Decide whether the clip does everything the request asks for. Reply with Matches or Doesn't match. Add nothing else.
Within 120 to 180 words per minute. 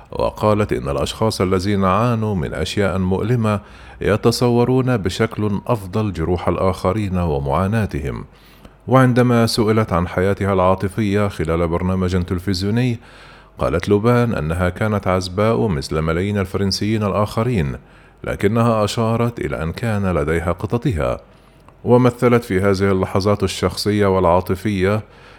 Doesn't match